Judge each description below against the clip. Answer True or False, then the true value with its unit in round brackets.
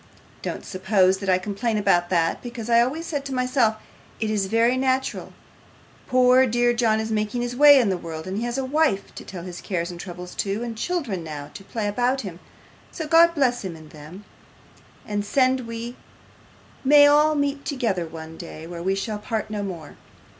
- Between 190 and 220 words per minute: True (195 wpm)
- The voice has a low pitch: False (220 Hz)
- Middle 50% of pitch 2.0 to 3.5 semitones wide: False (5.5 semitones)